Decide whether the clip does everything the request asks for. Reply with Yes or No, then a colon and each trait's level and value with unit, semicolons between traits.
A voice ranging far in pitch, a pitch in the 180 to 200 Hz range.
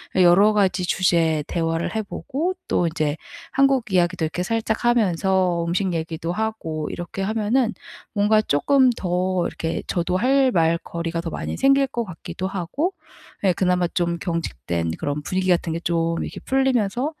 No: average, 4.7 semitones; medium, 185 Hz